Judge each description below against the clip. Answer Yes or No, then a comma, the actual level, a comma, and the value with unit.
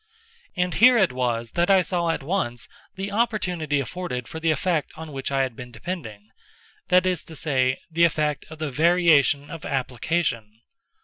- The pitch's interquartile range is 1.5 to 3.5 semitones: No, wide, 5.5 semitones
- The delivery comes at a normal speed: Yes, average, 170 wpm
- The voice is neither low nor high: Yes, medium, 155 Hz